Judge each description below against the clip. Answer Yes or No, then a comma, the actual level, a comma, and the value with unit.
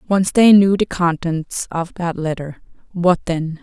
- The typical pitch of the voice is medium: Yes, medium, 175 Hz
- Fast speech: No, average, 150 wpm